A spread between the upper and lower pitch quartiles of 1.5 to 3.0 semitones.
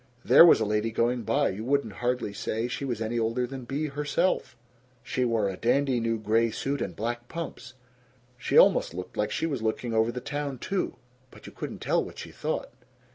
No: average, 3.6 semitones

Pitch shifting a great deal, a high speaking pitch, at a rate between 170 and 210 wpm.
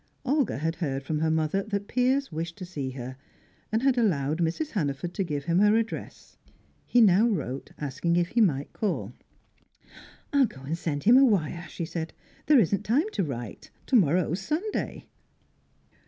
No: wide, 6.7 semitones; medium, 175 Hz; average, 175 wpm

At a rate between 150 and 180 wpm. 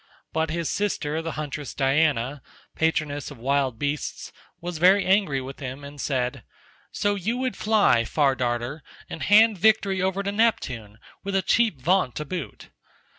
Yes: average, 160 wpm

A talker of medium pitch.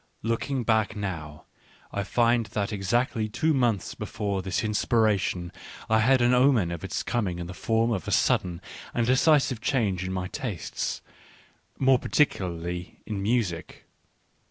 No: low, 110 Hz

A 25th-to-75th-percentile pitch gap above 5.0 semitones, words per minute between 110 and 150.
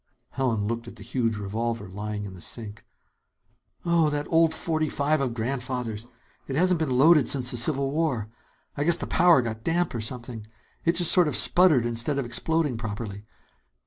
No: wide, 5.6 semitones; average, 180 wpm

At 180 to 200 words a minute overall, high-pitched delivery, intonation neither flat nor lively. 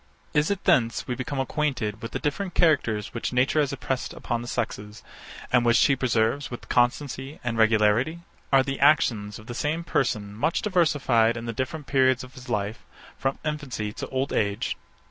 No: average, 185 wpm; low, 125 Hz; average, 4.2 semitones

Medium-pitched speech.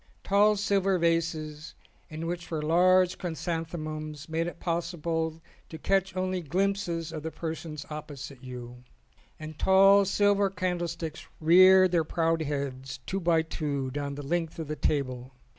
Yes: medium, 165 Hz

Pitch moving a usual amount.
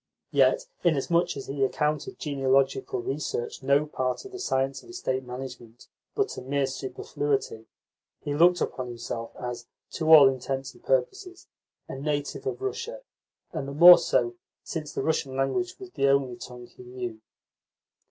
Yes: average, 4.0 semitones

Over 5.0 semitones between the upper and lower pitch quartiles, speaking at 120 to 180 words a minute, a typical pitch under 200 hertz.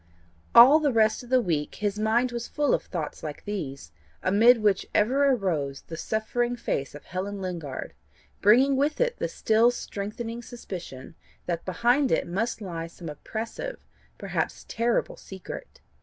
No: wide, 5.5 semitones; average, 155 wpm; high, 215 Hz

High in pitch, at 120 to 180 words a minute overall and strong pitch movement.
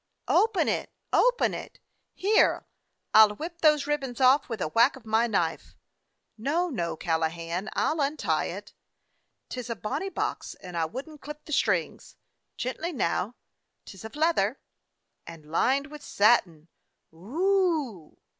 Yes: very high, 250 Hz; average, 155 wpm; wide, 8.0 semitones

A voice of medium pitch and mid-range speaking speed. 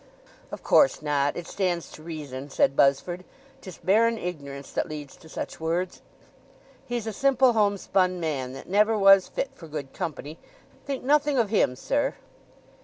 Yes: medium, 180 Hz; average, 155 wpm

